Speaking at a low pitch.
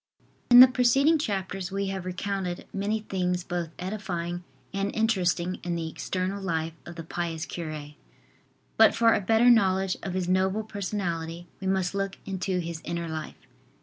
No: medium, 185 Hz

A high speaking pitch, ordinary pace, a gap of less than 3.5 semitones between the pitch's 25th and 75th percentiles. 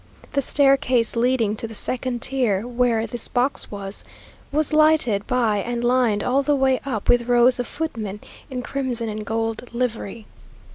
Yes: high, 245 Hz; average, 160 wpm; narrow, 2.6 semitones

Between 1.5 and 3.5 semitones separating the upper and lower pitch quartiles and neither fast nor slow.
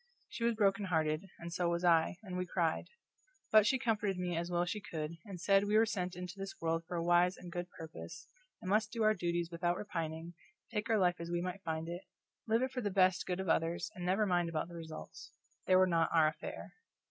No: average, 2.8 semitones; fast, 240 wpm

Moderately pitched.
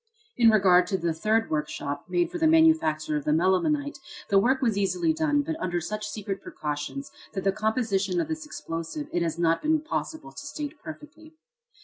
No: high, 215 Hz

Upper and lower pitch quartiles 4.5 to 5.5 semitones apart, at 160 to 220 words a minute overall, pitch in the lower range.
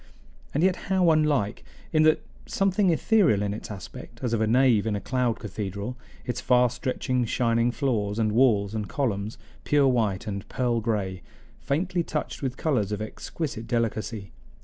Yes: average, 4.8 semitones; average, 165 wpm; low, 120 Hz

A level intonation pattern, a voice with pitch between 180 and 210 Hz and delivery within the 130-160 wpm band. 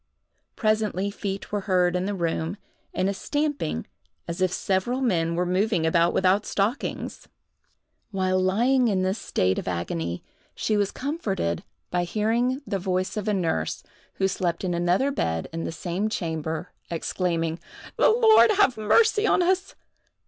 No: average, 4.1 semitones; high, 190 Hz; average, 155 wpm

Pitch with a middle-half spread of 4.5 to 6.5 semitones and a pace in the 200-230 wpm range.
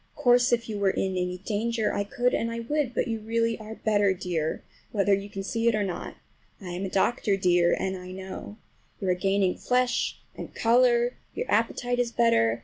No: average, 3.7 semitones; fast, 205 wpm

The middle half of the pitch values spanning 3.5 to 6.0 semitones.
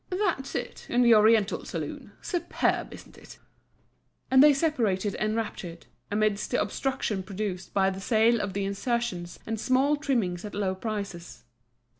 Yes: average, 4.3 semitones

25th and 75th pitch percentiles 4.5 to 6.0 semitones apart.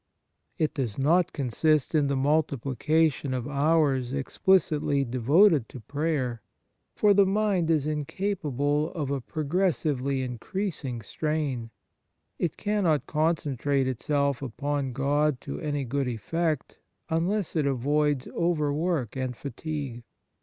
No: average, 3.3 semitones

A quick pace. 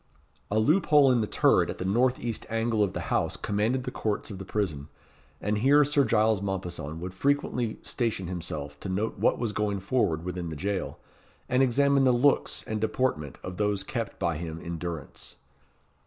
No: average, 190 wpm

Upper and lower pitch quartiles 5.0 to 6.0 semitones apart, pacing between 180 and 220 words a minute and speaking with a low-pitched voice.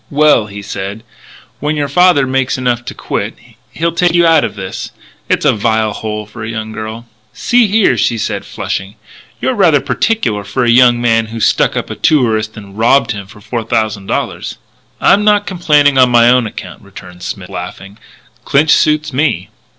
Yes: wide, 5.6 semitones; average, 190 wpm; low, 120 Hz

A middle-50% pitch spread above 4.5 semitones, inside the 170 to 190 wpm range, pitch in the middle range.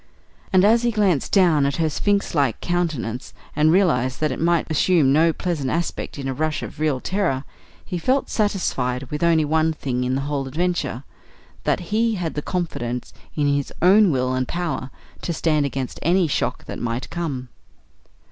Yes: average, 4.9 semitones; average, 175 wpm; medium, 155 Hz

